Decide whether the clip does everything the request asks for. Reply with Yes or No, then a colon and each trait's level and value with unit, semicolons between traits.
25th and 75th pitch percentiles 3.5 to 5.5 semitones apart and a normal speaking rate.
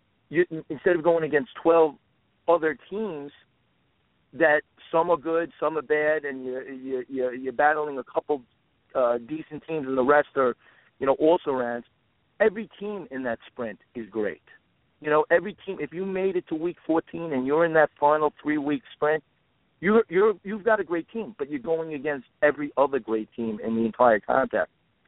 Yes: average, 4.5 semitones; average, 185 wpm